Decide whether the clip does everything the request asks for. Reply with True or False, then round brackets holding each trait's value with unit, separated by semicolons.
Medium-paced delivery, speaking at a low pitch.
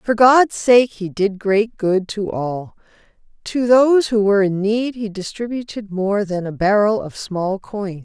False (180 wpm; 210 Hz)